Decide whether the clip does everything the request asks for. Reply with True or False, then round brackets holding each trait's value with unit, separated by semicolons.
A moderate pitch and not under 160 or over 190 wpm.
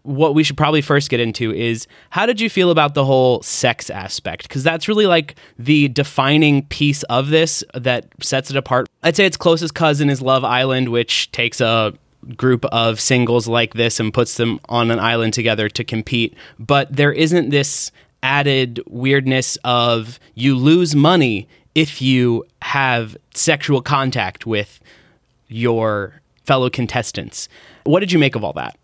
False (130 Hz; 170 wpm)